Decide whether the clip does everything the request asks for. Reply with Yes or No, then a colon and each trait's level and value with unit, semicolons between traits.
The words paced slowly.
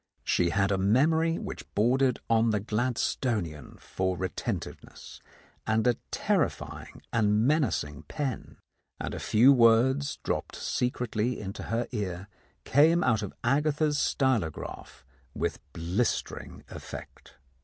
Yes: slow, 115 wpm